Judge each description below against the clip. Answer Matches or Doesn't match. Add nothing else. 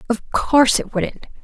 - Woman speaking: Matches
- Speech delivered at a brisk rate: Doesn't match